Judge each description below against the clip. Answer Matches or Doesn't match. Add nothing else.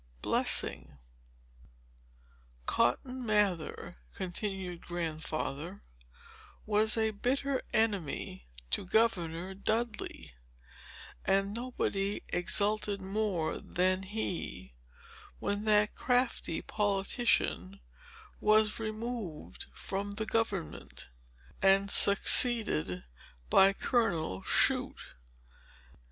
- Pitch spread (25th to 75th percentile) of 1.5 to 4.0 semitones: Matches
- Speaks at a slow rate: Matches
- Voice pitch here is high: Matches